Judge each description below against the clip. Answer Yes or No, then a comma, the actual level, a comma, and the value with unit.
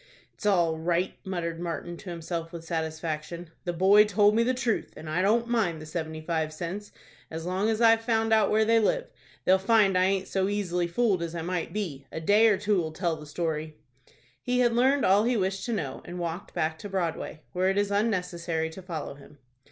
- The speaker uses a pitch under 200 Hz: Yes, medium, 185 Hz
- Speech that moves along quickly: Yes, fast, 215 wpm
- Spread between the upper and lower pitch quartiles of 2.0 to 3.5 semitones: No, average, 4.2 semitones